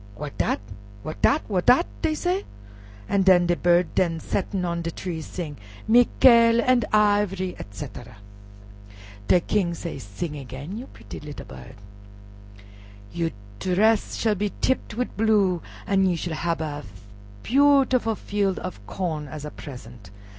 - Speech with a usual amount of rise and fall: No, wide, 5.7 semitones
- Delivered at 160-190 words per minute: No, average, 145 wpm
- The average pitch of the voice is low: No, medium, 180 Hz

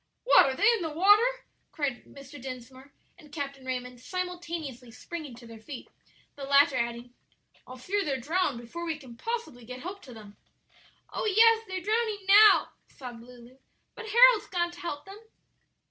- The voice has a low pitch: No, very high, 290 Hz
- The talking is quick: No, average, 170 wpm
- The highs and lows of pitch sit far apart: Yes, wide, 7.5 semitones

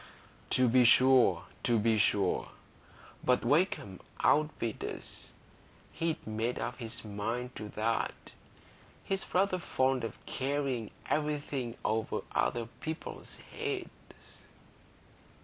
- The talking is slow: Yes, slow, 105 wpm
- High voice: No, low, 125 Hz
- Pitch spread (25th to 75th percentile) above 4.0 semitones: Yes, average, 4.7 semitones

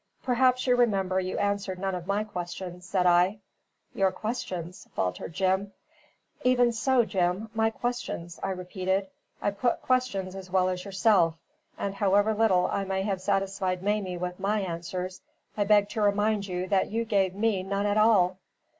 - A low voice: No, high, 195 Hz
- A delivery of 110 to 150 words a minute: No, average, 165 wpm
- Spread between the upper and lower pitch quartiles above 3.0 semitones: No, narrow, 2.5 semitones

